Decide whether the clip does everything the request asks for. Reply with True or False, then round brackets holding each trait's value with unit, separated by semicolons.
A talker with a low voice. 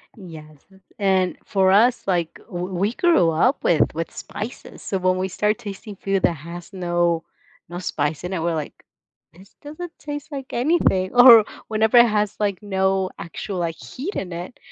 False (190 Hz)